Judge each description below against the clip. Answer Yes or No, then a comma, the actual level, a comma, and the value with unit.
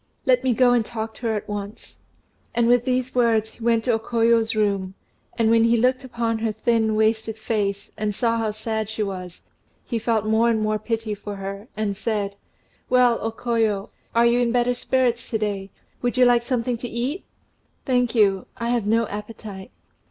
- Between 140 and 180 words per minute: No, average, 195 wpm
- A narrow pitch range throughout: Yes, narrow, 2.0 semitones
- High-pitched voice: Yes, high, 225 Hz